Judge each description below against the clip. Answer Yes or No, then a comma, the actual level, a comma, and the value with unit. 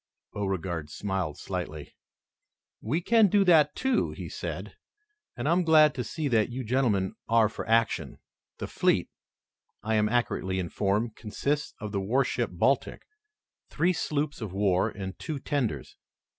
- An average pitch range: No, wide, 7.2 semitones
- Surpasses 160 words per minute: No, average, 145 wpm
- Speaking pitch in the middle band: No, low, 115 Hz